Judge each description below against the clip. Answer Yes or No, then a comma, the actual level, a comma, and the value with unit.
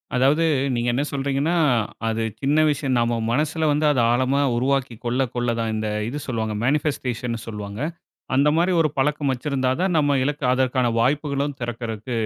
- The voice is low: Yes, low, 130 Hz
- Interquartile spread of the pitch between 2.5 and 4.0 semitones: Yes, average, 3.5 semitones